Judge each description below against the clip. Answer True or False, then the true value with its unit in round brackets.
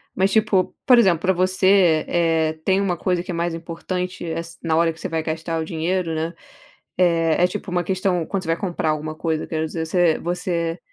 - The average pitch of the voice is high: False (170 Hz)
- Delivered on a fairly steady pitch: True (2.2 semitones)